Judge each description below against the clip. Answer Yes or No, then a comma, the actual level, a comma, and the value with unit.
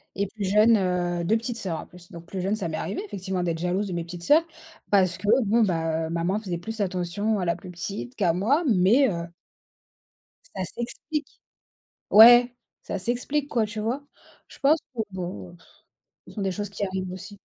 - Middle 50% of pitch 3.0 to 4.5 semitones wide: Yes, average, 4.0 semitones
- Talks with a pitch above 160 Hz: Yes, high, 190 Hz